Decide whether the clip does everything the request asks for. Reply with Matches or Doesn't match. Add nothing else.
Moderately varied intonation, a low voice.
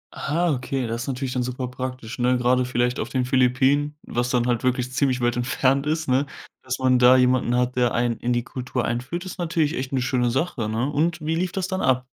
Doesn't match